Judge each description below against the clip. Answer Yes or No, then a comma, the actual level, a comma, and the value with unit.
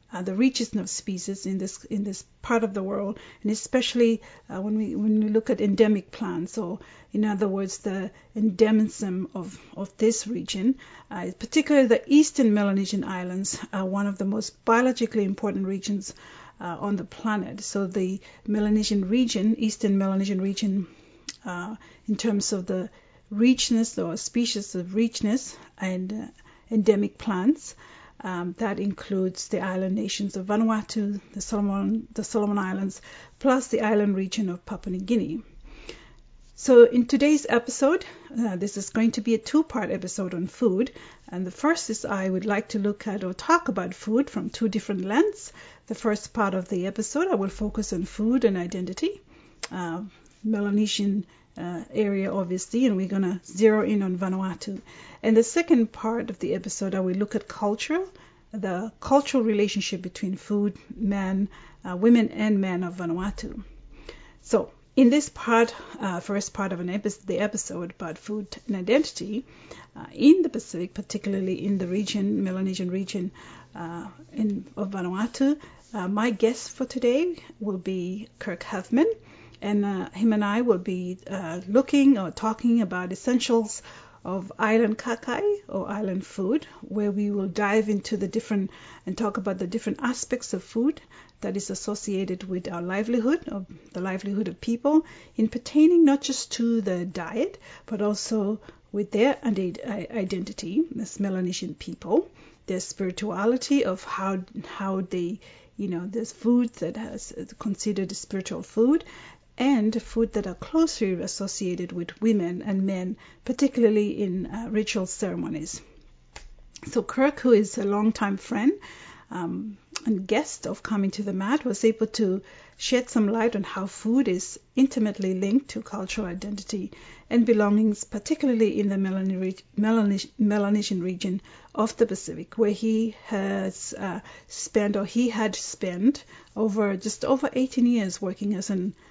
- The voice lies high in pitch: Yes, high, 210 Hz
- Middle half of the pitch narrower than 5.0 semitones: Yes, average, 3.0 semitones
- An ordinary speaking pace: Yes, average, 160 wpm